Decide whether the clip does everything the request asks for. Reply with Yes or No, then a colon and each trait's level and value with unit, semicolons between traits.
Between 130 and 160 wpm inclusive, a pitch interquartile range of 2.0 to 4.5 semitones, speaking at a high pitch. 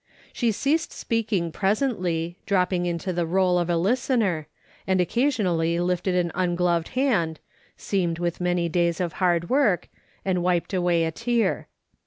No: average, 145 wpm; average, 3.2 semitones; medium, 180 Hz